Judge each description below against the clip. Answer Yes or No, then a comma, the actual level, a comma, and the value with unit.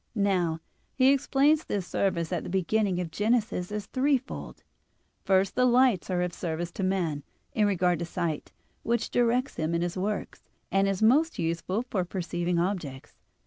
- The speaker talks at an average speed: Yes, average, 165 wpm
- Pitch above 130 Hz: Yes, high, 190 Hz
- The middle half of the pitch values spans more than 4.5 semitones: Yes, average, 5.2 semitones